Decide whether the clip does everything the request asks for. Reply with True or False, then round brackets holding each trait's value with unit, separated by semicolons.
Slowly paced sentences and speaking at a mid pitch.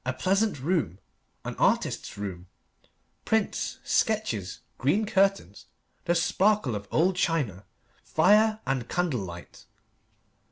True (110 wpm; 165 Hz)